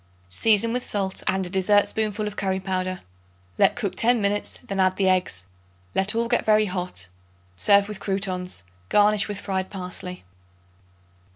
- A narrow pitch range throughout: Yes, narrow, 2.2 semitones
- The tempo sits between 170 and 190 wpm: No, average, 155 wpm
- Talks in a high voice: Yes, high, 195 Hz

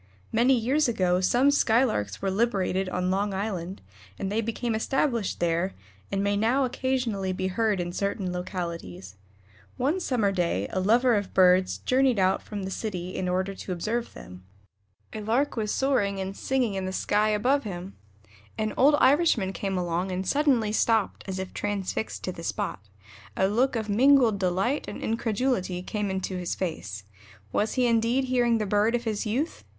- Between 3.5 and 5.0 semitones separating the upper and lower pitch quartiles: Yes, average, 4.3 semitones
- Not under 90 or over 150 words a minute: No, average, 175 wpm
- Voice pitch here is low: No, high, 205 Hz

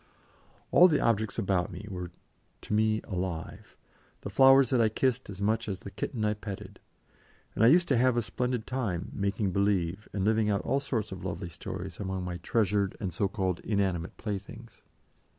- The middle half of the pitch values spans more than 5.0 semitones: No, average, 3.3 semitones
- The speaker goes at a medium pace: Yes, average, 185 wpm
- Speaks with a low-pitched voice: Yes, low, 105 Hz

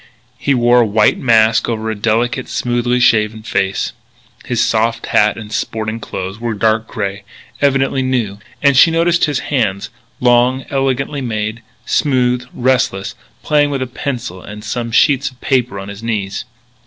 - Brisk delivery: No, average, 155 wpm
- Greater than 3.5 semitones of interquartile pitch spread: No, average, 3.2 semitones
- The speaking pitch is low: Yes, low, 120 Hz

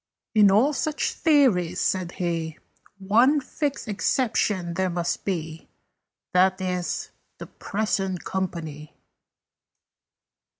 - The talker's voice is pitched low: No, high, 190 Hz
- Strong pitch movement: No, average, 3.9 semitones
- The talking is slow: Yes, slow, 95 wpm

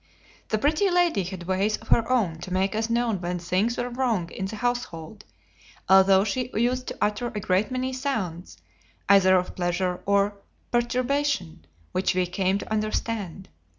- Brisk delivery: No, average, 165 wpm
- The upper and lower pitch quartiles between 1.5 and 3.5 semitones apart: No, average, 4.6 semitones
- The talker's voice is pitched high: Yes, high, 205 Hz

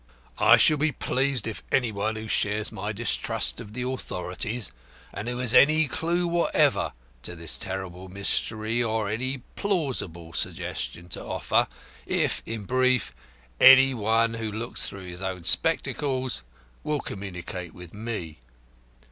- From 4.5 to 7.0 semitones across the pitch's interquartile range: Yes, average, 5.1 semitones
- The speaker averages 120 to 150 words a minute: Yes, average, 140 wpm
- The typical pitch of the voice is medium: No, low, 110 Hz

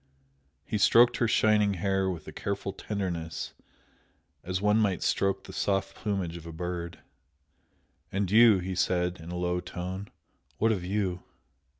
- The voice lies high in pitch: No, very low, 95 Hz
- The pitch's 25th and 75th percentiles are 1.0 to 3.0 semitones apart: Yes, narrow, 2.5 semitones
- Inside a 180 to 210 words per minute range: No, average, 155 wpm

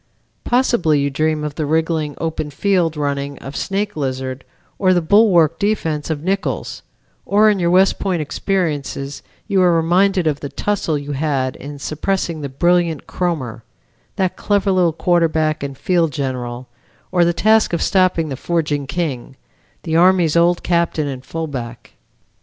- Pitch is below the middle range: No, medium, 160 Hz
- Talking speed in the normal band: Yes, average, 155 wpm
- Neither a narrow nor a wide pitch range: Yes, average, 4.1 semitones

